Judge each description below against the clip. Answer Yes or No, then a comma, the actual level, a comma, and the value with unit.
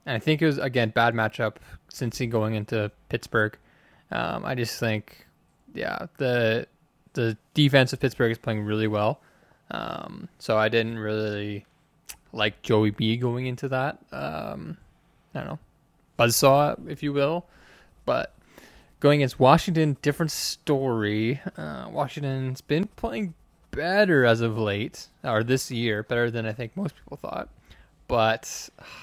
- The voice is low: Yes, low, 120 Hz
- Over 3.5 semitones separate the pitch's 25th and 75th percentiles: Yes, average, 4.4 semitones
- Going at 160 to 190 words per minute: No, average, 150 wpm